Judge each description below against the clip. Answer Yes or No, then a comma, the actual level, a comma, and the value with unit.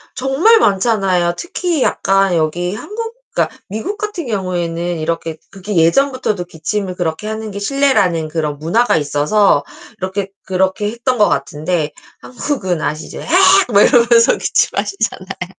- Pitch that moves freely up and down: Yes, wide, 6.0 semitones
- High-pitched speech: Yes, high, 195 Hz